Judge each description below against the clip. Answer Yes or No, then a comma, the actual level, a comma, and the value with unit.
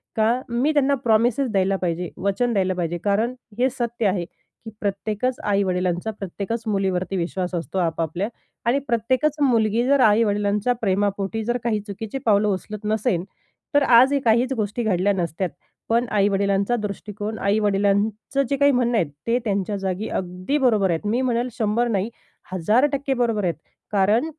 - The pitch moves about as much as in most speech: Yes, average, 3.6 semitones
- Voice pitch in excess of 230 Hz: No, high, 210 Hz